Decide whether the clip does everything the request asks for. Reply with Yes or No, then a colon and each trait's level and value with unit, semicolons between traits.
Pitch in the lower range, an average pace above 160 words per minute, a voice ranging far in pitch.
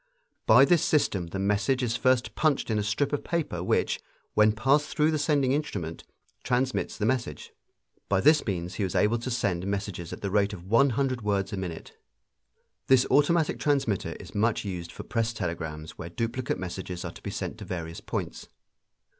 Yes: low, 110 Hz; average, 190 wpm; wide, 5.8 semitones